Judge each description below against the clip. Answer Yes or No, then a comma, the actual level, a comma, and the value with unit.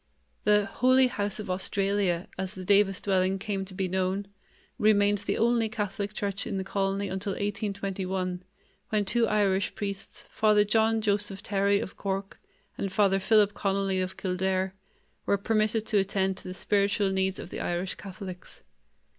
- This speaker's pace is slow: No, average, 160 wpm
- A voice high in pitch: Yes, high, 200 Hz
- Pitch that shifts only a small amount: Yes, narrow, 1.4 semitones